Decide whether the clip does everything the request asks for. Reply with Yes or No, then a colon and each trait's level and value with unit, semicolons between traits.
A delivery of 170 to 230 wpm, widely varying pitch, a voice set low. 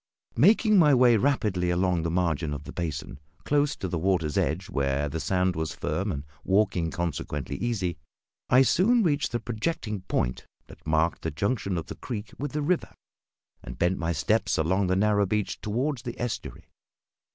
Yes: average, 180 wpm; wide, 6.6 semitones; very low, 95 Hz